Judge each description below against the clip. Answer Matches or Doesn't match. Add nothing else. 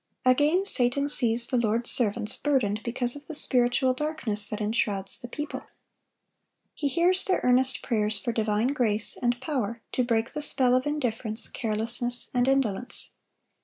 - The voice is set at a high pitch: Matches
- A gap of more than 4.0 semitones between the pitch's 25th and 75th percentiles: Doesn't match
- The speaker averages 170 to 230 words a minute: Doesn't match